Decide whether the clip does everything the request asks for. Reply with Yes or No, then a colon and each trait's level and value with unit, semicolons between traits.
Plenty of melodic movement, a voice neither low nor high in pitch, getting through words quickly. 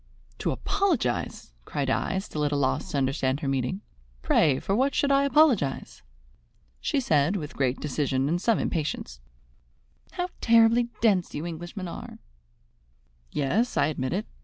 No: wide, 8.8 semitones; medium, 165 Hz; average, 155 wpm